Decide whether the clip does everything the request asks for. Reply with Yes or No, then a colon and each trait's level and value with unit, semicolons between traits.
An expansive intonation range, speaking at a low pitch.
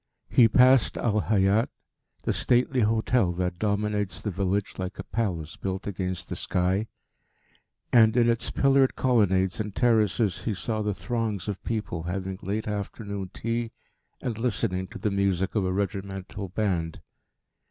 No: average, 3.2 semitones; low, 100 Hz